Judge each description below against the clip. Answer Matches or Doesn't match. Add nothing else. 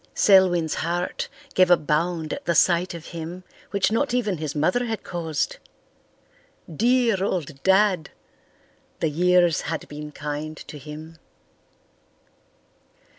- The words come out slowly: Matches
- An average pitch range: Matches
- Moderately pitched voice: Matches